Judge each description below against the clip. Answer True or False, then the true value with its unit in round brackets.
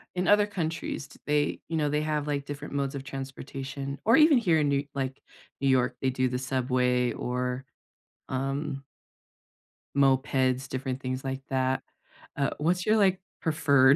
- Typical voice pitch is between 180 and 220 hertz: False (135 Hz)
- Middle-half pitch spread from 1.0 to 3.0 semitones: True (2.4 semitones)